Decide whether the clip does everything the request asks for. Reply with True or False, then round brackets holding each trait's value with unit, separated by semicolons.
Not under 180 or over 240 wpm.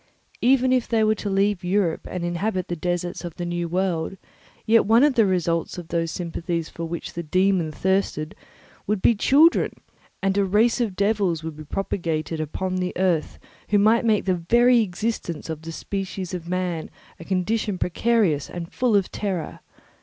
True (185 wpm)